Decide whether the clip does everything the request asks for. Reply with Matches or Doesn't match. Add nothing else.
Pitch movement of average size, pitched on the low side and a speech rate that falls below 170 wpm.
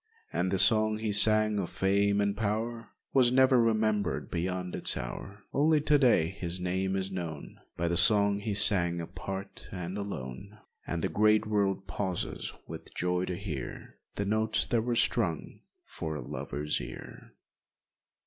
Matches